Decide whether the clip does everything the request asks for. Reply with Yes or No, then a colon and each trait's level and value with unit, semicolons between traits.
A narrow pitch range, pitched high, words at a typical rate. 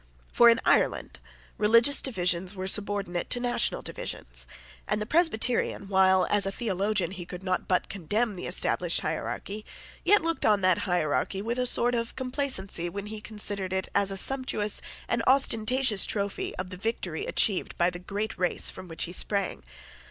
No: average, 3.8 semitones; high, 205 Hz; average, 170 wpm